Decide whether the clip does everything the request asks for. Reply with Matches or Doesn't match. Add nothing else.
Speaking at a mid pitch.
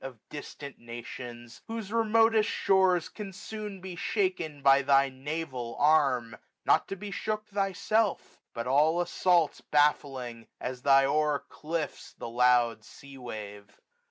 Matches